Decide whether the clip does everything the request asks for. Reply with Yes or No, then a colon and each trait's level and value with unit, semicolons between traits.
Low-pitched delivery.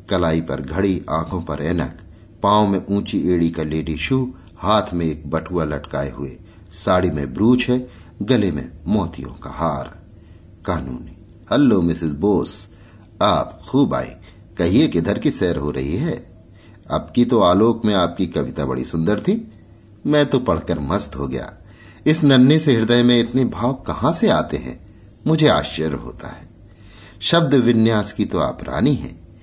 Yes: very low, 95 Hz